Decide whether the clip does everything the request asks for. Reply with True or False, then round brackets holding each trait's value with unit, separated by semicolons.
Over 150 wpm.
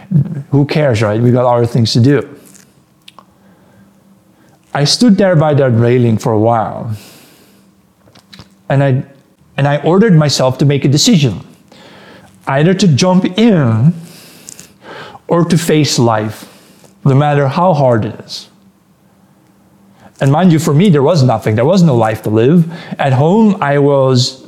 False (145 wpm)